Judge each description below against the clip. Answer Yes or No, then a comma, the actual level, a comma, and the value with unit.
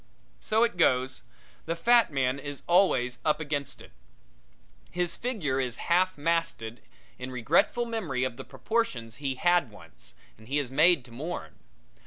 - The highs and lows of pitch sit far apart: Yes, wide, 5.7 semitones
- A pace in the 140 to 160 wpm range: Yes, average, 155 wpm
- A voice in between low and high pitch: Yes, medium, 145 Hz